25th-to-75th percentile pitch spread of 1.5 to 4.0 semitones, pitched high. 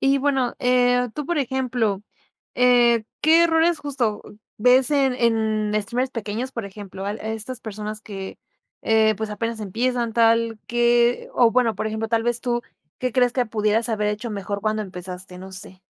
Yes: average, 2.8 semitones; high, 230 Hz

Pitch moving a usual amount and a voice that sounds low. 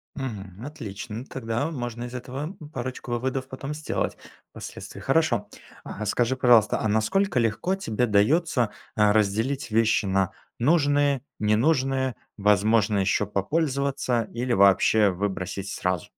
Yes: average, 4.4 semitones; low, 120 Hz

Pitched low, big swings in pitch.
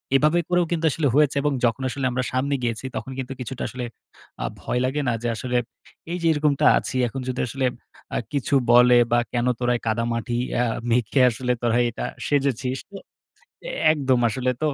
No: low, 130 Hz; average, 2.7 semitones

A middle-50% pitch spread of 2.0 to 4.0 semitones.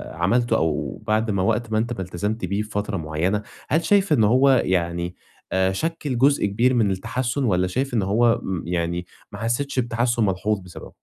No: average, 4.4 semitones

